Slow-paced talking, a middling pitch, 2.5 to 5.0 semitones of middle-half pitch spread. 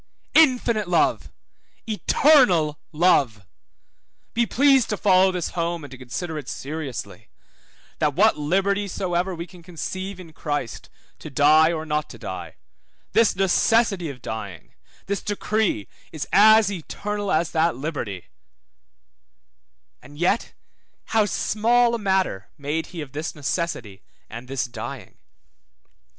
No: slow, 130 wpm; medium, 170 Hz; wide, 5.6 semitones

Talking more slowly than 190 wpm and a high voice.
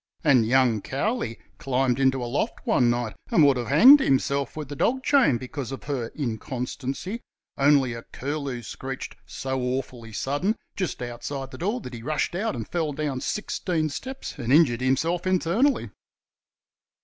No: average, 160 wpm; low, 135 Hz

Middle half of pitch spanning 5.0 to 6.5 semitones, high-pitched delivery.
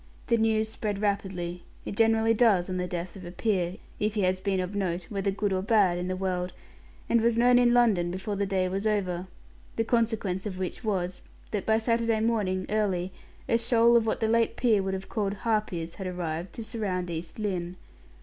No: average, 3.4 semitones; high, 200 Hz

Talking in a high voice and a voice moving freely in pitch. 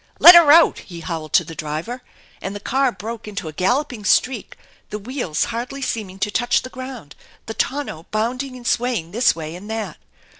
Yes: high, 220 Hz; wide, 5.9 semitones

